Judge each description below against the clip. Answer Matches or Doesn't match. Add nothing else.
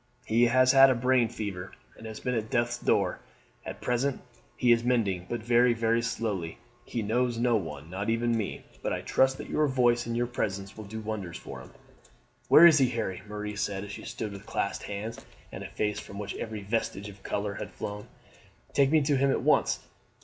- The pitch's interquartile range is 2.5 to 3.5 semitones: Matches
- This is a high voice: Doesn't match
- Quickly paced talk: Matches